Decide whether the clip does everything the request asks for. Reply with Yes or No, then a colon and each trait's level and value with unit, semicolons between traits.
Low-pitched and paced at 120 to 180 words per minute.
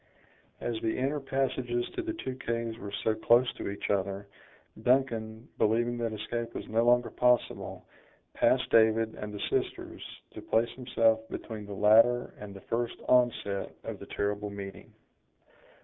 Yes: low, 115 Hz; average, 155 wpm